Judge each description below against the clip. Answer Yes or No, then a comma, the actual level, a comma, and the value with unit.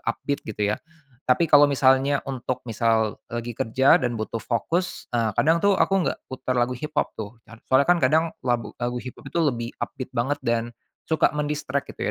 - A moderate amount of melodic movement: Yes, average, 3.7 semitones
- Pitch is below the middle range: Yes, low, 130 Hz